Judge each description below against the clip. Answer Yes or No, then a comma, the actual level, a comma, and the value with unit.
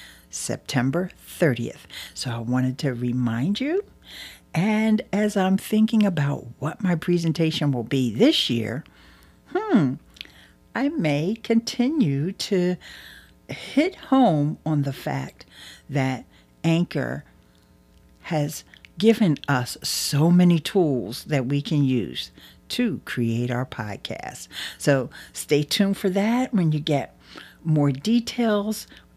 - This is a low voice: No, medium, 160 Hz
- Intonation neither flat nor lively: No, wide, 7.8 semitones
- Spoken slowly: Yes, slow, 115 wpm